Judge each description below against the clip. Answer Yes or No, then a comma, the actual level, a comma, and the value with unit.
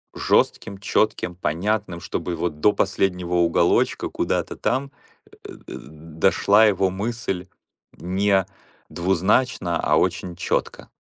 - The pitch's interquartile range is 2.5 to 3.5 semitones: Yes, average, 2.9 semitones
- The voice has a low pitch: Yes, very low, 95 Hz